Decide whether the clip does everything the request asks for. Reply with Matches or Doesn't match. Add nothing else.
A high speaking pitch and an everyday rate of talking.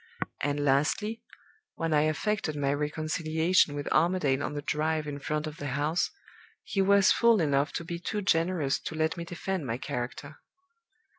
Doesn't match